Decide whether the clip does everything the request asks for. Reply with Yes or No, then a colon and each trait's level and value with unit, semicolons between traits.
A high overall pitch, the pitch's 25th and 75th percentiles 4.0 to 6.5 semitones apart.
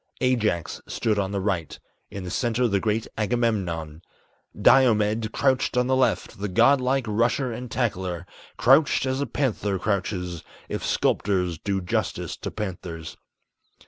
No: low, 105 Hz; average, 4.9 semitones